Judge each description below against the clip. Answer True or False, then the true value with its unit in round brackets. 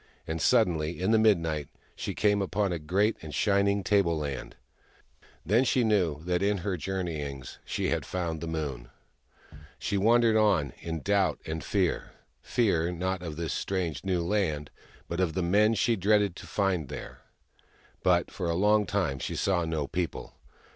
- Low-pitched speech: True (90 Hz)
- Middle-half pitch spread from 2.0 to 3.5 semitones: False (4.0 semitones)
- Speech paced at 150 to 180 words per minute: True (170 wpm)